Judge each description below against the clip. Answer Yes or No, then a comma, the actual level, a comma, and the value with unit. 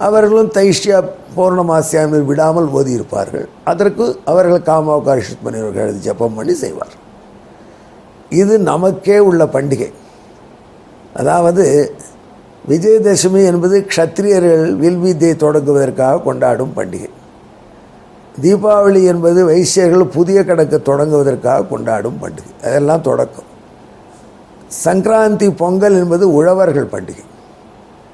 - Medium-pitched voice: Yes, medium, 175 Hz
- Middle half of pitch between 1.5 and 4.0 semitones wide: No, average, 4.4 semitones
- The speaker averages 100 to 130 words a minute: No, average, 85 wpm